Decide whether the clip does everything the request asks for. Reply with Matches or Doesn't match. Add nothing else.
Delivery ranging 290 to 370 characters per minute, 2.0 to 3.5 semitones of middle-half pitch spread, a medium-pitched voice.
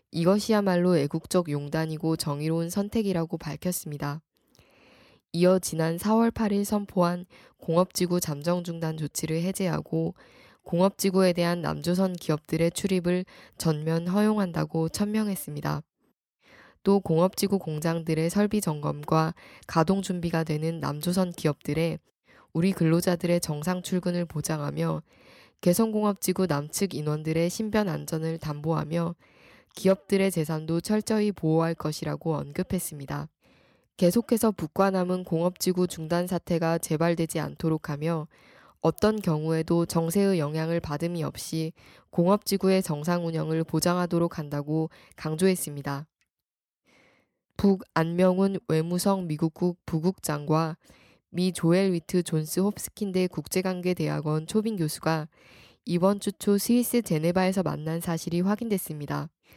Matches